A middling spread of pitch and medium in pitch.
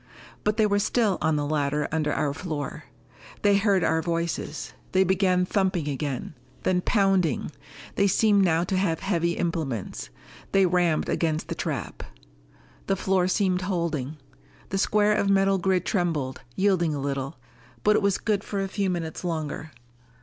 Yes: average, 3.7 semitones; medium, 180 Hz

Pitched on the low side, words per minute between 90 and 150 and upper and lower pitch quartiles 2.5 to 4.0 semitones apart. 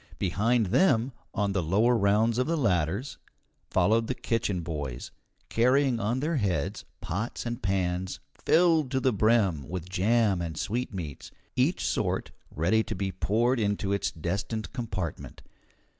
No: low, 105 Hz; average, 145 wpm; average, 4.6 semitones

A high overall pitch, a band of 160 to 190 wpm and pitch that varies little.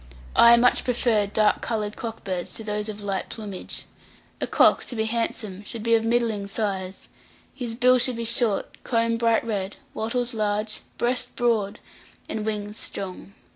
Yes: high, 220 Hz; average, 165 wpm; narrow, 2.1 semitones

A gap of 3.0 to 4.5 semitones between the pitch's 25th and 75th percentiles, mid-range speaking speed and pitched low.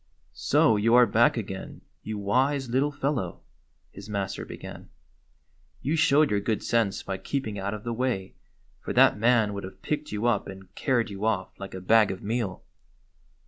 Yes: average, 4.0 semitones; average, 185 wpm; low, 110 Hz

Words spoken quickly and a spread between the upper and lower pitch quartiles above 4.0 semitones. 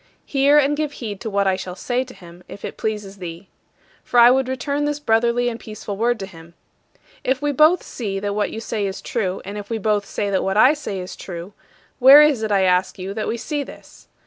Yes: fast, 240 wpm; average, 5.0 semitones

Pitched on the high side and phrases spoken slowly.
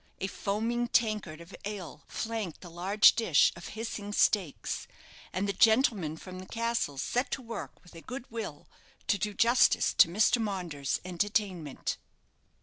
No: high, 200 Hz; average, 150 wpm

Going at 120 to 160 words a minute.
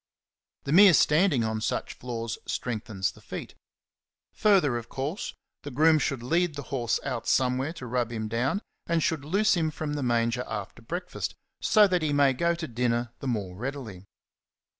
No: average, 175 wpm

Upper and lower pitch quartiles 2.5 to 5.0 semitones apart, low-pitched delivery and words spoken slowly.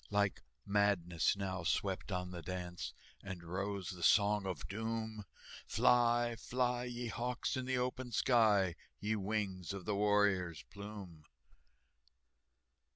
Yes: average, 3.5 semitones; low, 100 Hz; slow, 125 wpm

